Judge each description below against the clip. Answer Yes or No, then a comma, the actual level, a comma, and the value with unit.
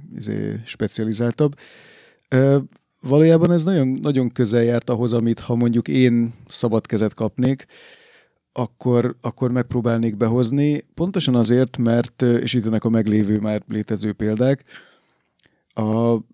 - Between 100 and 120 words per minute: Yes, average, 110 wpm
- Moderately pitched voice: No, low, 120 Hz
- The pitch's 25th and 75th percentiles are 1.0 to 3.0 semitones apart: Yes, narrow, 2.5 semitones